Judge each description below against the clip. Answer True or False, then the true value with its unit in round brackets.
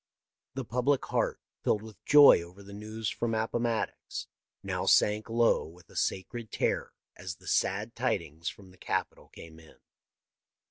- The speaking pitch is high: False (105 Hz)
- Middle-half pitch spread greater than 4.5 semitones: False (4.2 semitones)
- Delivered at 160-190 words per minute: False (150 wpm)